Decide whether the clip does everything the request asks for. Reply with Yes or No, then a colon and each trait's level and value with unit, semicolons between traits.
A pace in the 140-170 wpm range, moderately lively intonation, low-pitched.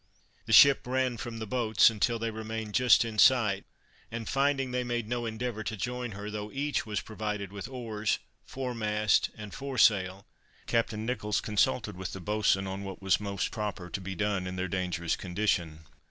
No: average, 180 wpm; average, 3.3 semitones; low, 110 Hz